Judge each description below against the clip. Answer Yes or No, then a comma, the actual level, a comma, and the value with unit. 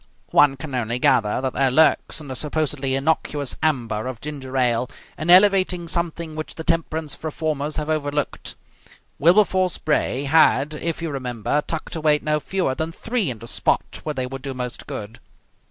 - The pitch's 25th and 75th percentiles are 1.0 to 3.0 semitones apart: No, average, 3.4 semitones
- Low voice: No, medium, 150 Hz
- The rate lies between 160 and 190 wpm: Yes, average, 170 wpm